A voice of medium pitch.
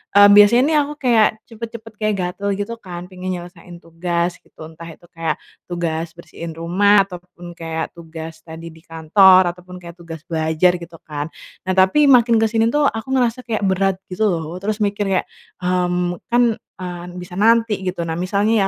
Yes: medium, 180 Hz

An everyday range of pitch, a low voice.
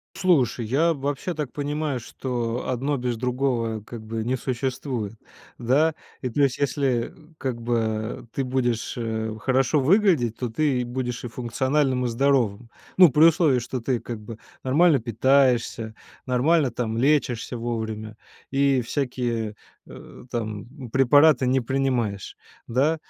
Yes: average, 3.1 semitones; low, 125 Hz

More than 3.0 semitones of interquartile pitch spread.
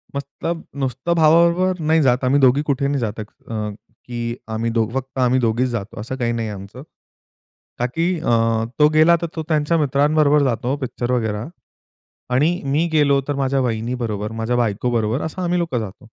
Yes: average, 4.4 semitones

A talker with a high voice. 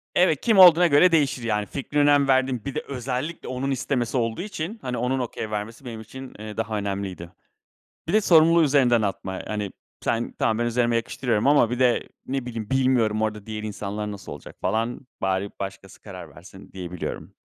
No: low, 120 Hz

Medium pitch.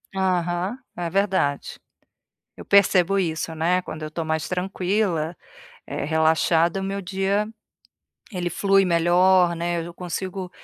Yes: medium, 180 Hz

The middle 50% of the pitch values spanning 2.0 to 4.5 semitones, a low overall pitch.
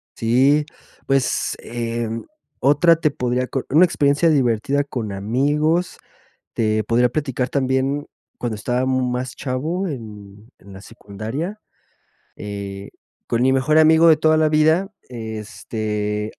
No: average, 5.0 semitones; low, 130 Hz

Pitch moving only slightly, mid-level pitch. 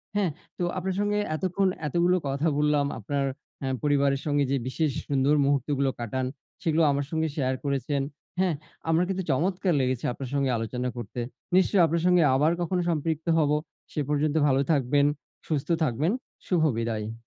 No: average, 3.8 semitones; medium, 145 Hz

